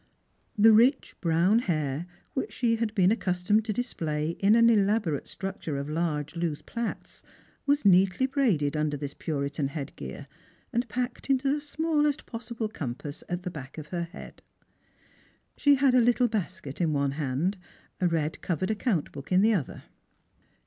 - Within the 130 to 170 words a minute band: Yes, average, 165 wpm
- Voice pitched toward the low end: No, medium, 185 Hz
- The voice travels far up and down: Yes, wide, 7.3 semitones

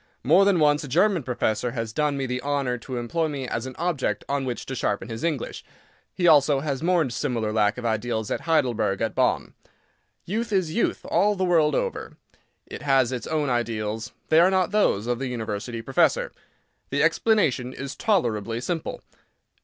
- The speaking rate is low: No, average, 185 wpm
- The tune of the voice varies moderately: No, wide, 5.8 semitones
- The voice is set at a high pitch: No, low, 135 Hz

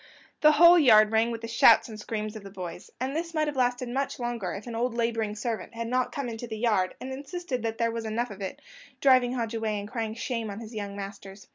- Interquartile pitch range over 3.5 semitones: No, average, 2.9 semitones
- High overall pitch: Yes, high, 230 Hz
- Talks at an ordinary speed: No, fast, 250 wpm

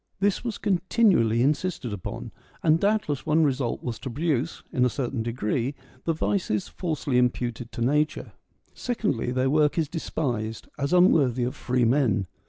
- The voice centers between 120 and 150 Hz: Yes, medium, 140 Hz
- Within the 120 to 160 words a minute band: Yes, average, 155 wpm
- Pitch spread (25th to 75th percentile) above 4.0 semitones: Yes, average, 5.2 semitones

